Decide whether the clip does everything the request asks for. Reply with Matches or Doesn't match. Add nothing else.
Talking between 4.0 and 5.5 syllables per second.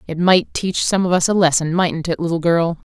Matches